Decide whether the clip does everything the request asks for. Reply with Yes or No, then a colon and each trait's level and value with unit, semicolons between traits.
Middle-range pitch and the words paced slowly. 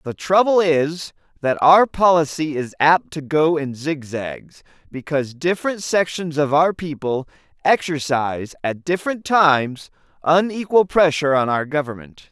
Yes: medium, 155 Hz; slow, 130 wpm